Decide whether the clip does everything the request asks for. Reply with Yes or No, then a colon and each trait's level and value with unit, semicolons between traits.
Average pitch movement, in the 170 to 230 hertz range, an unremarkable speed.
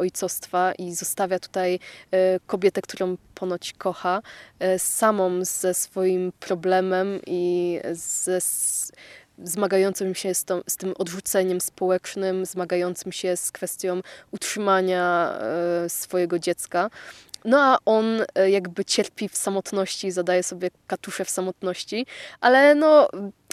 No: narrow, 1.3 semitones; medium, 185 Hz; average, 120 wpm